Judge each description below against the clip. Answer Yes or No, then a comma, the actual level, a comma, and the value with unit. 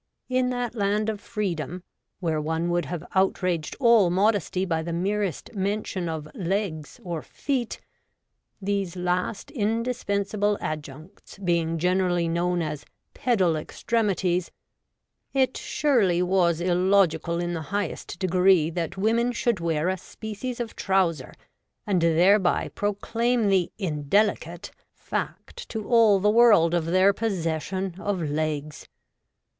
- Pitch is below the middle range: No, medium, 185 Hz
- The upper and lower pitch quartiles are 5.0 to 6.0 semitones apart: No, average, 3.7 semitones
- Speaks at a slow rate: Yes, slow, 130 wpm